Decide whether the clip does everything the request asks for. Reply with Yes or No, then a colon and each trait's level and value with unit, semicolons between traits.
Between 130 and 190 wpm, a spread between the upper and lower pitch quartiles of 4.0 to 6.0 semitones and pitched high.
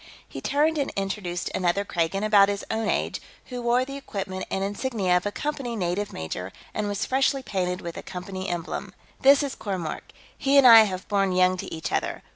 No: average, 200 wpm; average, 5.0 semitones; high, 200 Hz